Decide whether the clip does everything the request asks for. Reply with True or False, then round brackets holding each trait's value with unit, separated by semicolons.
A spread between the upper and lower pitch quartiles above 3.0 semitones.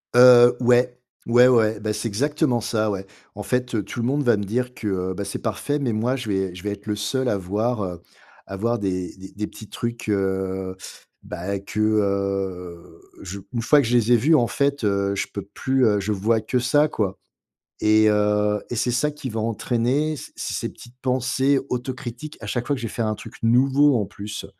True (3.7 semitones)